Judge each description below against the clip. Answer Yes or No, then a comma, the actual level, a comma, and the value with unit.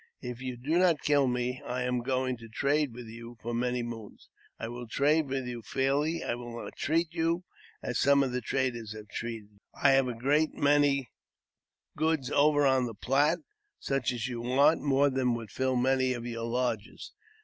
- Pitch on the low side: Yes, low, 130 Hz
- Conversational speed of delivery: Yes, average, 190 wpm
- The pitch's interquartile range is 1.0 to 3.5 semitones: Yes, average, 3.1 semitones